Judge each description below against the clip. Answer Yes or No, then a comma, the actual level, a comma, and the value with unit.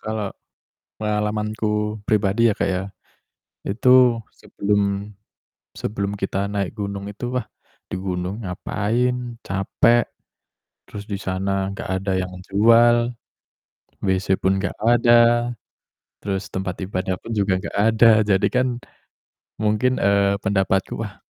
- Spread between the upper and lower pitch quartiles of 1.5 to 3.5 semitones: Yes, average, 2.9 semitones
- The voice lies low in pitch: Yes, low, 100 Hz